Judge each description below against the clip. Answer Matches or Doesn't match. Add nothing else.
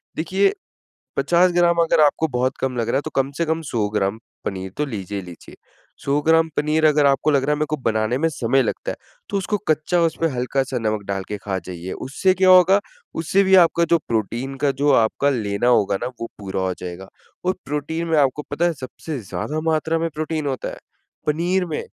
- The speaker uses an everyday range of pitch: Doesn't match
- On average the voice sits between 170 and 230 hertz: Doesn't match